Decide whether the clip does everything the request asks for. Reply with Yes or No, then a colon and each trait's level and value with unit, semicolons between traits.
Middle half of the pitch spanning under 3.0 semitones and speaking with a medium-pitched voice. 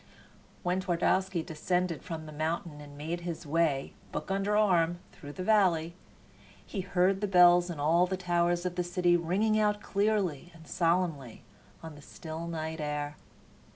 Yes: narrow, 2.5 semitones; medium, 175 Hz